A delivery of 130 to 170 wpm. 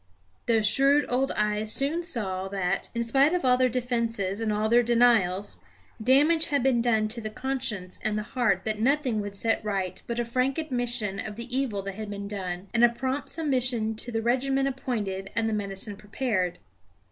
No: average, 195 wpm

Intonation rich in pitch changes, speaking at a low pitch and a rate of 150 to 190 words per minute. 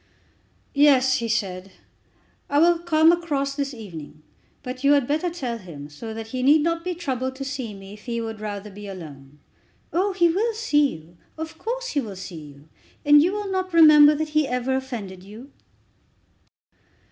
No: wide, 7.3 semitones; very high, 265 Hz; average, 180 wpm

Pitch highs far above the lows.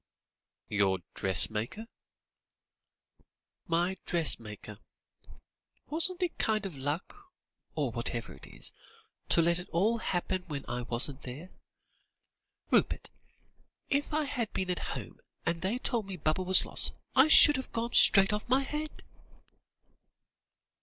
Yes: wide, 8.6 semitones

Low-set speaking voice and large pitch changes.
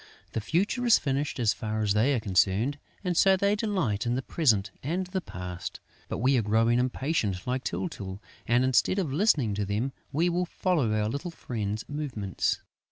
Yes: low, 130 Hz; wide, 7.7 semitones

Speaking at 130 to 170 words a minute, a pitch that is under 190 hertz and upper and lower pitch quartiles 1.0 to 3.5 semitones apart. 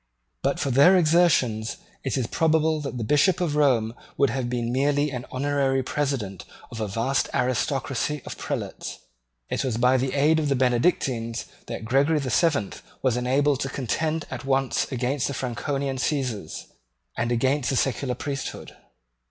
Yes: average, 160 wpm; low, 135 Hz; average, 2.8 semitones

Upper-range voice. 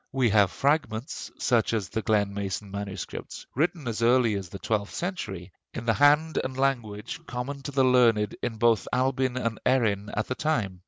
No: low, 115 Hz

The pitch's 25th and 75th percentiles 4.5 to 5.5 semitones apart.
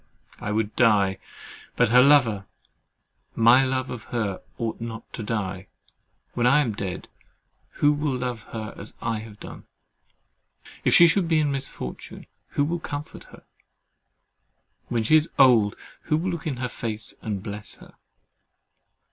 Yes: average, 5.0 semitones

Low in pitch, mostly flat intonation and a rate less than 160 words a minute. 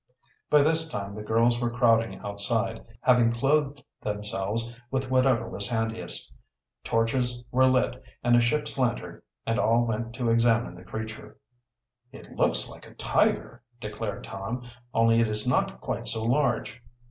Yes: low, 115 Hz; narrow, 2.0 semitones; average, 150 wpm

